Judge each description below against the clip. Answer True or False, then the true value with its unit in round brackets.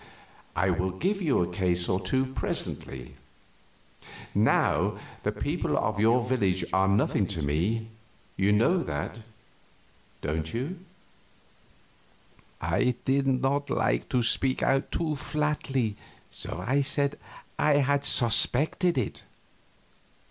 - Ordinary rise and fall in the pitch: False (6.9 semitones)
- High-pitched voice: False (120 Hz)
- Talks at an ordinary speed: False (120 wpm)